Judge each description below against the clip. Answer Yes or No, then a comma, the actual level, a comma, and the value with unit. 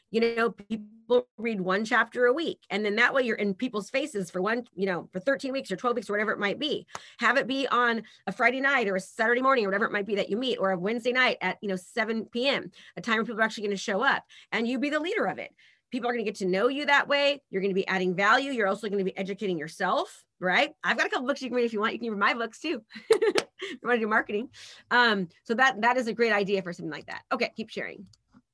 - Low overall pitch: No, high, 225 Hz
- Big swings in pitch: No, average, 4.0 semitones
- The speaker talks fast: Yes, fast, 290 wpm